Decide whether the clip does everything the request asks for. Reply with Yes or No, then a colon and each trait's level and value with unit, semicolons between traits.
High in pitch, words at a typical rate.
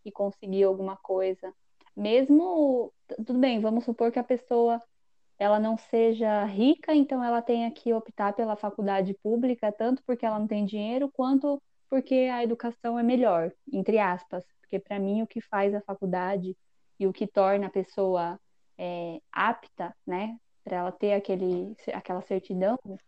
Yes: high, 215 Hz; average, 160 wpm